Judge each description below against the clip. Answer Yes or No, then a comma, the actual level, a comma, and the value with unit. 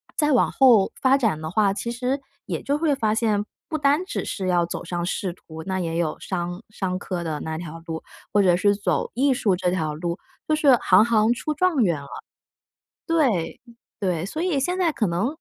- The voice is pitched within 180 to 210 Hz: Yes, high, 205 Hz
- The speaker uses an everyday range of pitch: No, wide, 7.6 semitones